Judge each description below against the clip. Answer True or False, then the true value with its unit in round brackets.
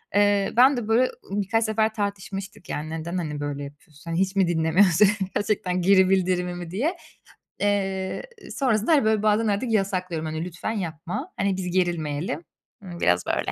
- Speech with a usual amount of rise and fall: True (3.5 semitones)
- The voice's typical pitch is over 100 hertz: True (190 Hz)